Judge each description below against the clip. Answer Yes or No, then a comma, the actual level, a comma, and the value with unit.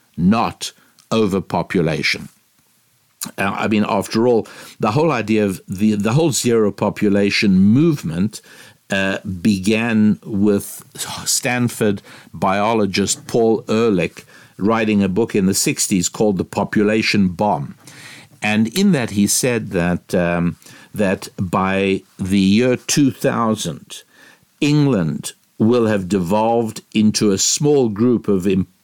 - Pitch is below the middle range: Yes, low, 105 Hz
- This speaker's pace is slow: Yes, slow, 120 wpm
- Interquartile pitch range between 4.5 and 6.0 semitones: No, average, 3.0 semitones